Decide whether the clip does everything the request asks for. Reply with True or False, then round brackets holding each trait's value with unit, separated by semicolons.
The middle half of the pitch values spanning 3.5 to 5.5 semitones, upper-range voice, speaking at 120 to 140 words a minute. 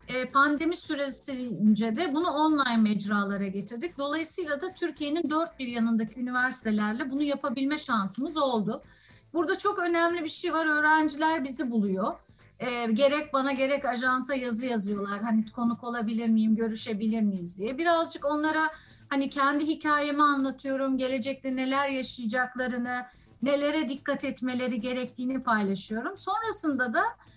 True (4.4 semitones; 270 Hz; 125 wpm)